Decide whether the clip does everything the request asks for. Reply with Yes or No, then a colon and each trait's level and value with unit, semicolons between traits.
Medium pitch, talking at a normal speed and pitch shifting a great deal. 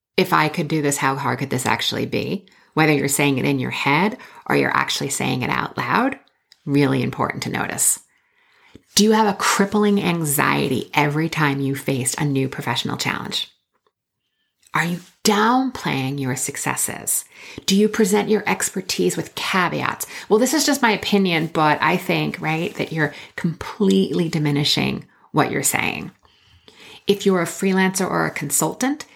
Yes: medium, 165 Hz; average, 165 wpm; wide, 5.9 semitones